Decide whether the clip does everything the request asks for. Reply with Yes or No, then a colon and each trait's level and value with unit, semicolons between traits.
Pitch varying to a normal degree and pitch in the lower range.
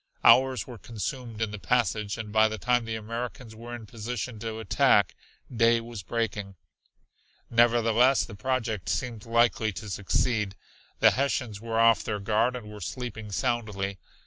No: narrow, 2.2 semitones; low, 115 Hz